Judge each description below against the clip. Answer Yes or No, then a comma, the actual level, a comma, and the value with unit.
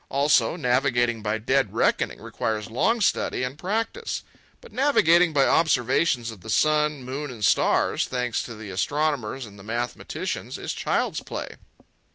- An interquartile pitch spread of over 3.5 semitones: Yes, average, 5.2 semitones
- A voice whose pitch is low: Yes, low, 130 Hz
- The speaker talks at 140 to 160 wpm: Yes, average, 145 wpm